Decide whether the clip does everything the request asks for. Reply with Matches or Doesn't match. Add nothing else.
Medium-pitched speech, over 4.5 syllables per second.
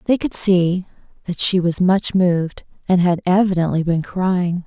Doesn't match